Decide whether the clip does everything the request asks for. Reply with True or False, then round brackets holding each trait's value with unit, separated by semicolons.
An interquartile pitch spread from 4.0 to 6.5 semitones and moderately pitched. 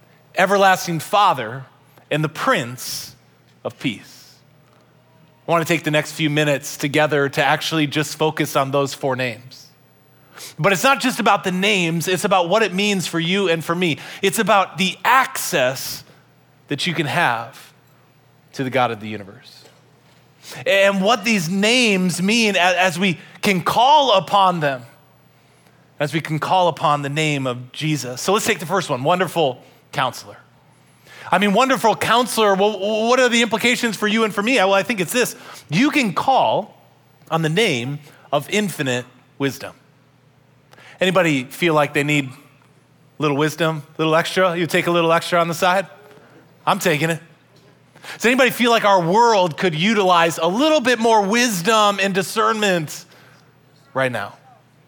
True (5.5 semitones; 165 Hz)